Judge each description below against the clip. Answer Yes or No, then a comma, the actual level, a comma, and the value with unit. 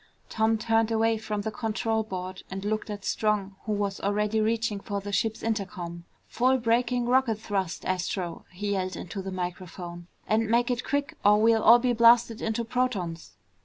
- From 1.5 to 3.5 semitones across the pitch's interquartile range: Yes, average, 2.8 semitones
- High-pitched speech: Yes, high, 215 Hz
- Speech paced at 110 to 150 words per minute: No, average, 175 wpm